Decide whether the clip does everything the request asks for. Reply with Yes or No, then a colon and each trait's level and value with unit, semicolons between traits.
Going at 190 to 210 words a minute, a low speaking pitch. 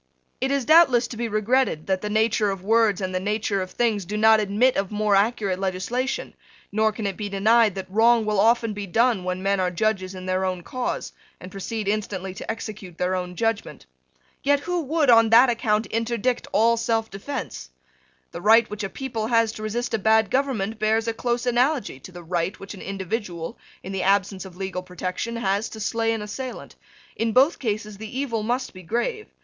No: average, 200 wpm; high, 215 Hz